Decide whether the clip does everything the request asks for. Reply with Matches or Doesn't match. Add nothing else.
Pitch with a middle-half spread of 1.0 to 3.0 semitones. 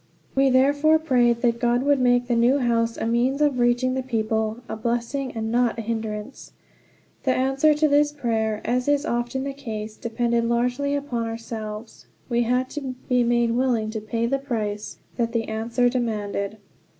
Matches